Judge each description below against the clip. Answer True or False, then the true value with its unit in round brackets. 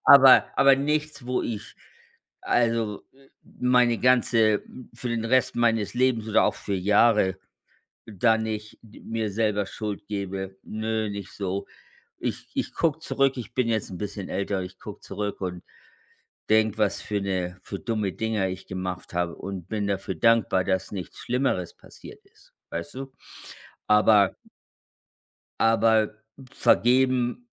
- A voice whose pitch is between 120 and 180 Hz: False (110 Hz)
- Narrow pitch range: False (3.3 semitones)